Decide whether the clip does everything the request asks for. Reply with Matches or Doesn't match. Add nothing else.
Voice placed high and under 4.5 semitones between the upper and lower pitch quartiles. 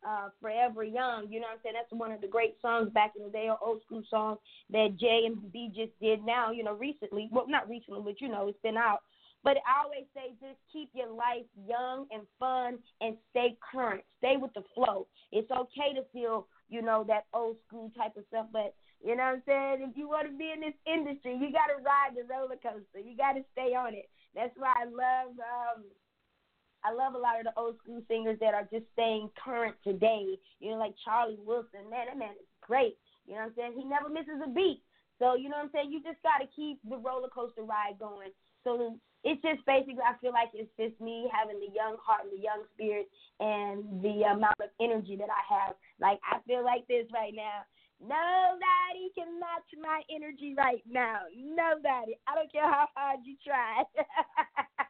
Matches